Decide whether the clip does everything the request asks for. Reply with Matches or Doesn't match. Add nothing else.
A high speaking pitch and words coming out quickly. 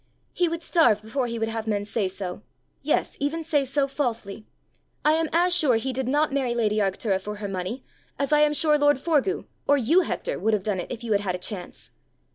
Matches